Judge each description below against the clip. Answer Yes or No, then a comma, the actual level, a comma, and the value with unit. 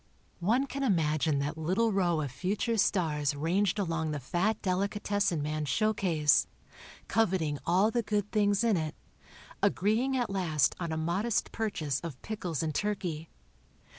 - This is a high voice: No, medium, 180 Hz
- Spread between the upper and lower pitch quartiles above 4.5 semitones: Yes, average, 5.1 semitones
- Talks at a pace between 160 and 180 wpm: No, average, 145 wpm